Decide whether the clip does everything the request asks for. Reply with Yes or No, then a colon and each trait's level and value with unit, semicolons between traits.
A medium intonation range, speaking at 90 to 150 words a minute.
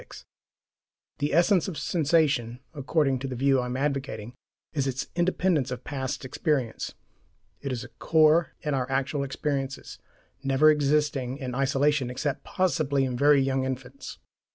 No: narrow, 2.3 semitones; average, 145 wpm